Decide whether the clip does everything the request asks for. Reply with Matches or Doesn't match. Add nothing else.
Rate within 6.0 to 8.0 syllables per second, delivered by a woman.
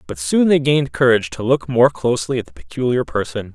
Doesn't match